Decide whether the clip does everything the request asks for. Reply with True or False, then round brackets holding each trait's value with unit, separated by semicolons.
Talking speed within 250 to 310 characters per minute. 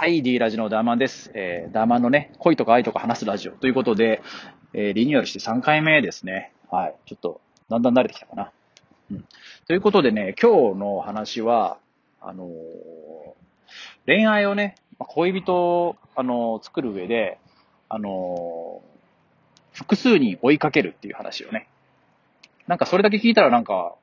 False (330 characters per minute)